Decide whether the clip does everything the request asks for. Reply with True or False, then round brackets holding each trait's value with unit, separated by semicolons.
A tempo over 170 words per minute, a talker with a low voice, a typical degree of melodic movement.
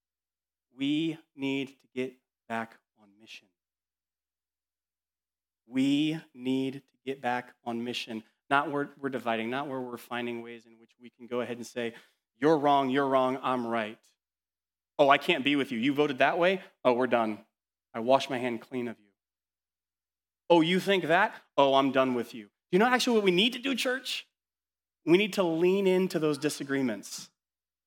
False (180 wpm; 125 Hz; 8.0 semitones)